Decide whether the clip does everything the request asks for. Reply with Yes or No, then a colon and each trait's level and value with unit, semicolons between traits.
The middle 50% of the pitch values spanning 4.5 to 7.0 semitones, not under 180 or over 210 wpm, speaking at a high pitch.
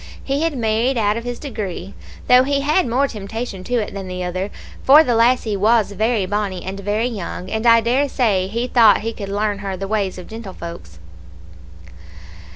No: average, 3.7 semitones; average, 190 wpm; high, 220 Hz